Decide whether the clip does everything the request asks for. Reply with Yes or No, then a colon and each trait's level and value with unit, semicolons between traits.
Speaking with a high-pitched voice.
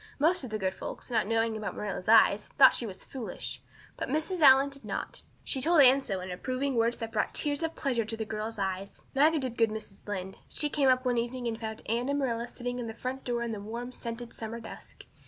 Yes: high, 235 Hz